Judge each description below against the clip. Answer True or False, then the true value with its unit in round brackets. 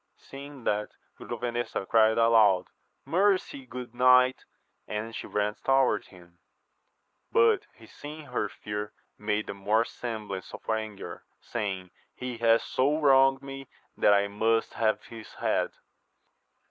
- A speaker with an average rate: False (130 wpm)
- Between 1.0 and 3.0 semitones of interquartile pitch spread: False (4.2 semitones)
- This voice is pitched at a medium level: False (115 Hz)